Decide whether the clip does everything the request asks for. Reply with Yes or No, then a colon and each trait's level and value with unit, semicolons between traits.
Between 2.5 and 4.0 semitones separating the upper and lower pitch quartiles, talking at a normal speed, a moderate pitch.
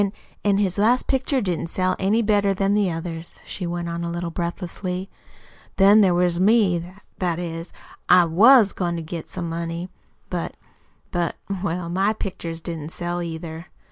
Yes: average, 2.8 semitones; average, 170 wpm; medium, 175 Hz